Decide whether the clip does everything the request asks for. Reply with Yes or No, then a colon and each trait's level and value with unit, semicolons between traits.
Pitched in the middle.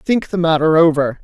Yes: medium, 165 Hz